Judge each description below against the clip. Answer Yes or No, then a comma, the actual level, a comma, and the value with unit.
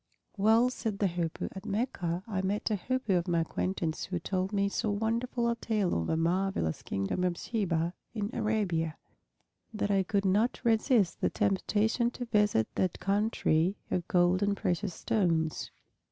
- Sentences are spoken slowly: No, average, 165 wpm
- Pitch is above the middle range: Yes, high, 195 Hz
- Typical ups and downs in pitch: Yes, average, 3.7 semitones